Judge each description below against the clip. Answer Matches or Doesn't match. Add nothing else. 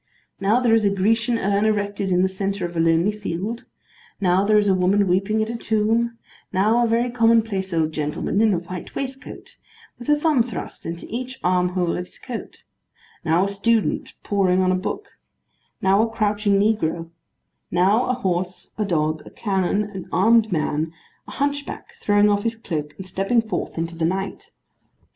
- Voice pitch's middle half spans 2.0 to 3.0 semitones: Doesn't match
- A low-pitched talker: Doesn't match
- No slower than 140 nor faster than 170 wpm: Doesn't match